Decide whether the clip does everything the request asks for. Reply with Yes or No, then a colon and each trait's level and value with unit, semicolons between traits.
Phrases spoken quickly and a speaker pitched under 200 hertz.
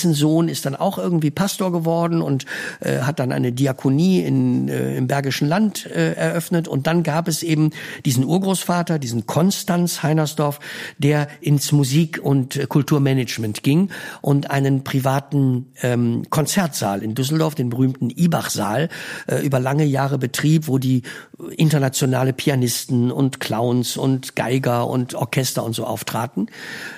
No: average, 145 wpm; medium, 140 Hz